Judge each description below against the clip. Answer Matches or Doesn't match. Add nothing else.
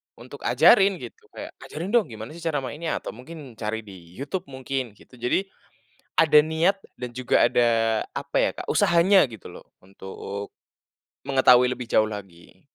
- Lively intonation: Matches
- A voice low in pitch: Matches